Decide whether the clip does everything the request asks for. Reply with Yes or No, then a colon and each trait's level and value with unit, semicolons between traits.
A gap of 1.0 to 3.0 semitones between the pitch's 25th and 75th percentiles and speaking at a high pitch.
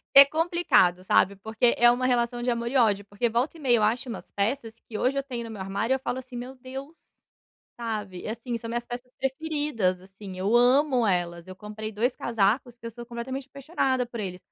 No: average, 3.6 semitones; high, 235 Hz